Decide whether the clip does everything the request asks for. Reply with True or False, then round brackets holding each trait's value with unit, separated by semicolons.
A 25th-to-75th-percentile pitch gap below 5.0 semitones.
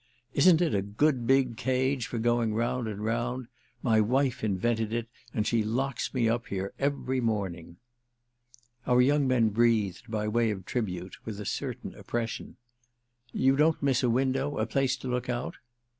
True (3.2 semitones)